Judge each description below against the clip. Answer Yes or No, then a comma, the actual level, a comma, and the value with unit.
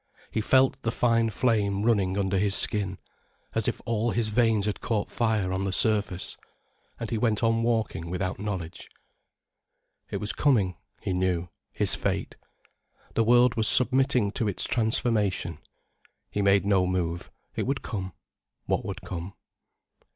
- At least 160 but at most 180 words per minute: No, average, 150 wpm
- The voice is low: Yes, low, 105 Hz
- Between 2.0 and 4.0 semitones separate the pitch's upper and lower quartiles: Yes, average, 3.4 semitones